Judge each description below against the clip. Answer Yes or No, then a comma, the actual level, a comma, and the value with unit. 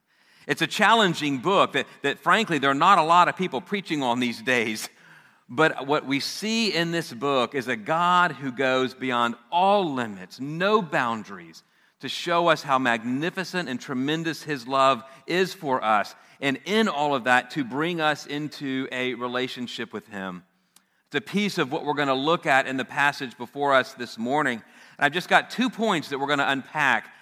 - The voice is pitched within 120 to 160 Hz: Yes, medium, 140 Hz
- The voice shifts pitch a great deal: No, average, 4.7 semitones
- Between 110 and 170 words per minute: No, average, 195 wpm